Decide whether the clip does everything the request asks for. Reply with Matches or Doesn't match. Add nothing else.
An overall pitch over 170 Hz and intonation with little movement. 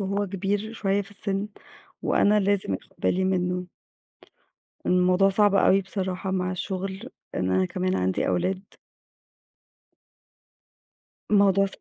Matches